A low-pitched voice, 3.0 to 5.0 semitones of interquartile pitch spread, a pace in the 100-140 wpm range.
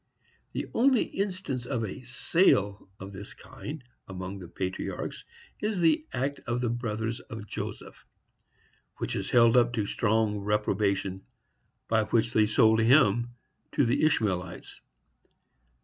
Yes: low, 115 Hz; average, 3.9 semitones; slow, 135 wpm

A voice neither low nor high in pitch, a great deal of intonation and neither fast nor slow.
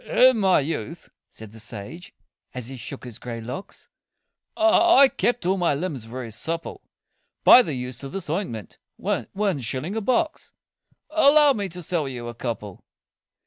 Yes: medium, 155 Hz; wide, 8.8 semitones; average, 160 wpm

